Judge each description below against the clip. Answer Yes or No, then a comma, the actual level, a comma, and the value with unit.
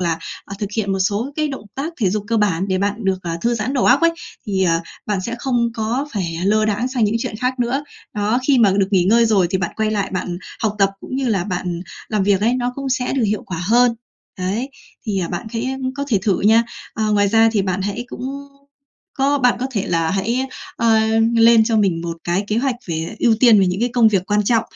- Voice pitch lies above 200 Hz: Yes, high, 215 Hz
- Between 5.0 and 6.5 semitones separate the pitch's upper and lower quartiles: No, average, 3.8 semitones